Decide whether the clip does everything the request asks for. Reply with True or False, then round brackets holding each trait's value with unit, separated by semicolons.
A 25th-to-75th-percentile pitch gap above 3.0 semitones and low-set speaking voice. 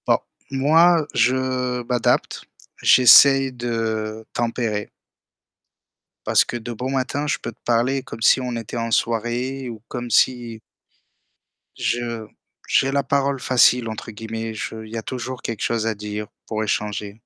False (2.6 semitones; 120 Hz)